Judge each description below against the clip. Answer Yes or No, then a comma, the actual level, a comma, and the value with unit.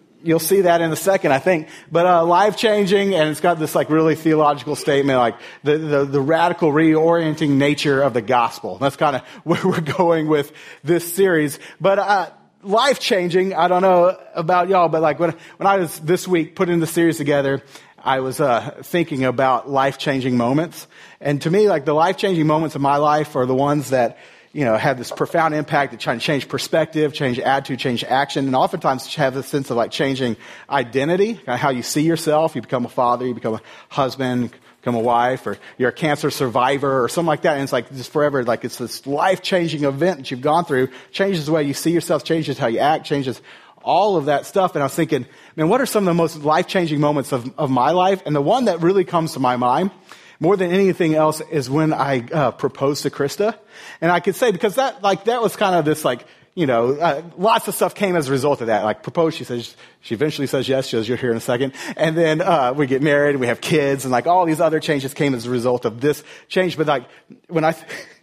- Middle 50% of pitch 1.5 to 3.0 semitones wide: No, average, 4.0 semitones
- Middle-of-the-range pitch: Yes, medium, 150 Hz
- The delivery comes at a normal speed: No, fast, 235 wpm